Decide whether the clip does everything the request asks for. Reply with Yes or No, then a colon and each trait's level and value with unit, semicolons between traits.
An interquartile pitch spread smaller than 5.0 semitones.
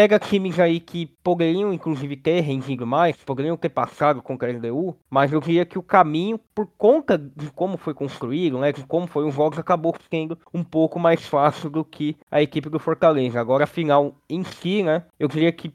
Yes: average, 2.9 semitones